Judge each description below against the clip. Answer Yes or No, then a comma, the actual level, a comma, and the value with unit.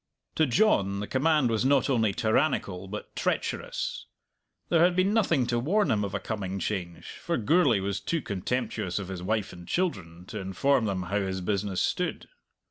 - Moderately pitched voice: No, low, 105 Hz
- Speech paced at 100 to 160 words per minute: No, average, 180 wpm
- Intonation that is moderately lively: No, wide, 6.6 semitones